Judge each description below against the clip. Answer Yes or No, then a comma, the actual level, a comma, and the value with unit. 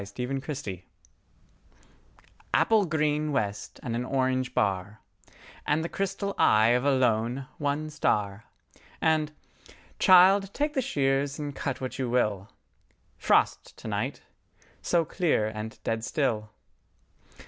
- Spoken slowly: Yes, slow, 120 wpm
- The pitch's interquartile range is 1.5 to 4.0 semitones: No, wide, 5.5 semitones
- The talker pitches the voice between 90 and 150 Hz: Yes, low, 135 Hz